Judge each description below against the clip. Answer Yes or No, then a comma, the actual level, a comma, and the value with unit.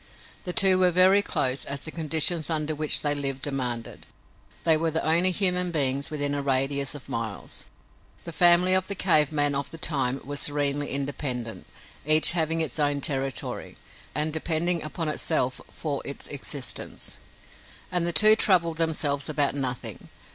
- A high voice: No, medium, 150 Hz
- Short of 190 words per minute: Yes, average, 160 wpm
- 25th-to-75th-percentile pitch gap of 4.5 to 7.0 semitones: No, average, 3.2 semitones